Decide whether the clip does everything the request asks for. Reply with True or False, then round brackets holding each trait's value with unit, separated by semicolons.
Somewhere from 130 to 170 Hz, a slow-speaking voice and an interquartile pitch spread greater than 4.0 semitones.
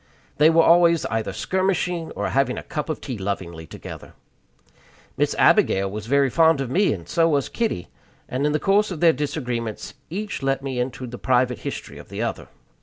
False (140 Hz; 190 wpm; 5.3 semitones)